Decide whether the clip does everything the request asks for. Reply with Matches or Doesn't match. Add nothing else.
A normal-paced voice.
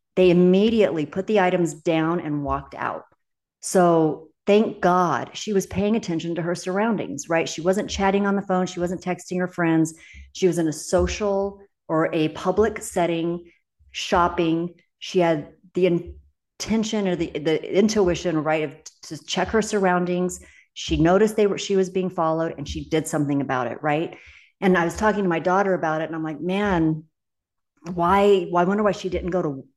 Matches